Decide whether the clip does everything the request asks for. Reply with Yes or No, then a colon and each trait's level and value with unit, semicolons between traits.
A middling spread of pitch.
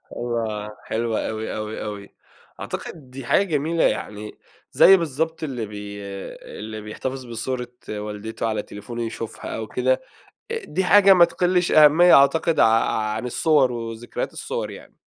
No: wide, 6.3 semitones